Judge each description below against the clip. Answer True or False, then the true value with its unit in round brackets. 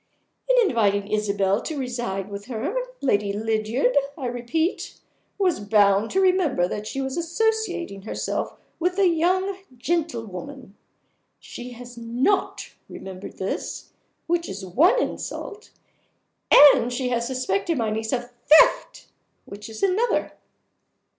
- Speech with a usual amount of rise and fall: False (8.2 semitones)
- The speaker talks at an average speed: False (125 wpm)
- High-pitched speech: True (245 Hz)